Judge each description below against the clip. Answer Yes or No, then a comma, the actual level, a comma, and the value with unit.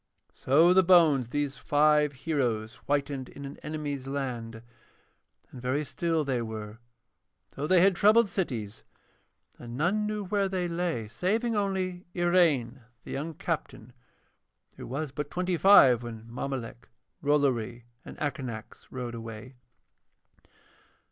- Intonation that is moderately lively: No, wide, 6.2 semitones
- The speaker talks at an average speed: No, slow, 130 wpm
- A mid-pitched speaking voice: Yes, medium, 145 Hz